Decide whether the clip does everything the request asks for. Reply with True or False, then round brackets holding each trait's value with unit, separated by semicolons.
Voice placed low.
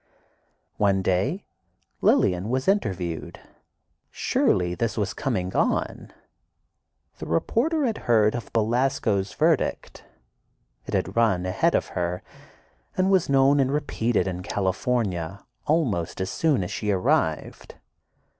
True (105 Hz)